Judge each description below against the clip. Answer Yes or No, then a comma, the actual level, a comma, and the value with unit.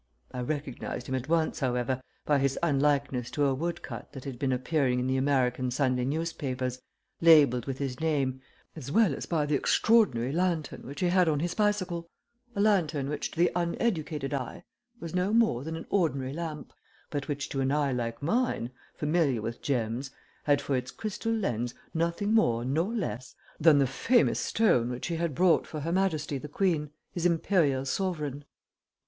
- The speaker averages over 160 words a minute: Yes, average, 180 wpm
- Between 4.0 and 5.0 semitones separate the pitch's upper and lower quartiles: Yes, average, 4.5 semitones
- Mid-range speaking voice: Yes, medium, 145 Hz